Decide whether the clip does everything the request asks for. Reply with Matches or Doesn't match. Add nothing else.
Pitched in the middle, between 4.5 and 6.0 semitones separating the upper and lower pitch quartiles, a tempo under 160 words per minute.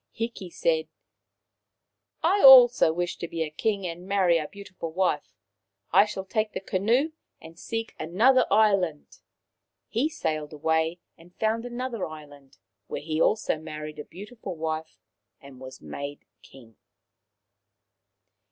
Matches